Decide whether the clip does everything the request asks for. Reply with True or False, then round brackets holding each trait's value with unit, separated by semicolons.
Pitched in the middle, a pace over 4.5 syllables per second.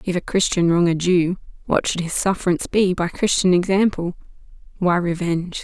True (175 Hz; 5.4 syllables/s)